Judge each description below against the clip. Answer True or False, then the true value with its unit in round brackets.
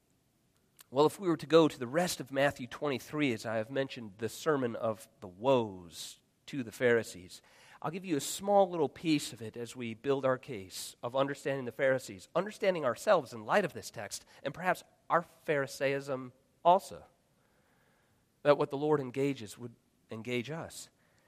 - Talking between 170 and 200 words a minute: True (175 wpm)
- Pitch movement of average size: True (4.2 semitones)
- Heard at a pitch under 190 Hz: True (135 Hz)